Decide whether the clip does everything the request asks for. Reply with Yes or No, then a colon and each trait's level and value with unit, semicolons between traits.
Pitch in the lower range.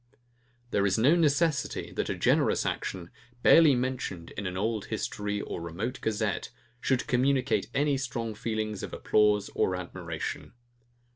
Yes: low, 110 Hz